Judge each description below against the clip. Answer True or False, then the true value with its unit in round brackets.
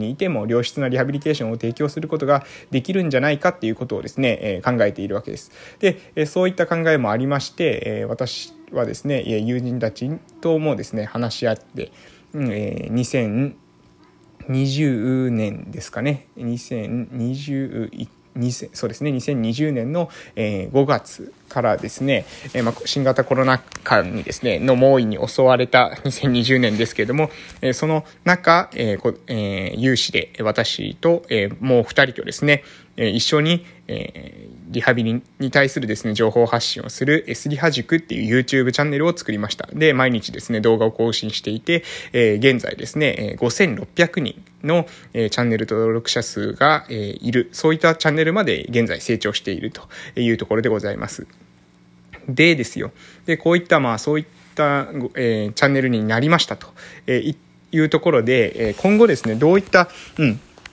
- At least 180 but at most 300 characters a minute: False (310 characters per minute)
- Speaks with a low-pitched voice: True (130 Hz)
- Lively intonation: False (5.0 semitones)